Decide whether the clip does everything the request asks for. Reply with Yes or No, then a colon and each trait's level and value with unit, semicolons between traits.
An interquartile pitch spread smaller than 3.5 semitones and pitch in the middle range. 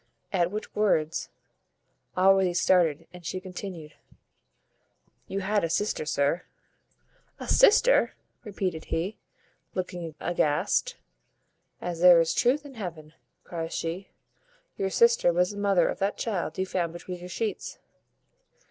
Yes: average, 3.1 semitones; medium, 180 Hz